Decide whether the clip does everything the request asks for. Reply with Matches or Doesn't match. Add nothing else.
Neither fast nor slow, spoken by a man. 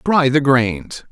Matches